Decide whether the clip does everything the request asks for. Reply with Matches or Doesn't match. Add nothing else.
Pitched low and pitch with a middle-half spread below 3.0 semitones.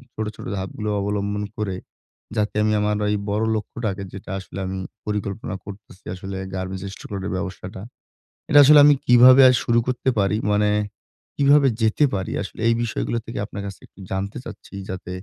Matches